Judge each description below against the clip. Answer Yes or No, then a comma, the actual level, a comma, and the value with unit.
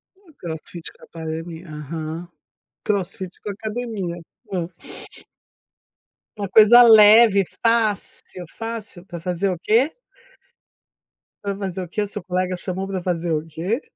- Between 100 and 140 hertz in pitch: No, medium, 185 Hz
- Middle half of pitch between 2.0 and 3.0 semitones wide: No, average, 3.7 semitones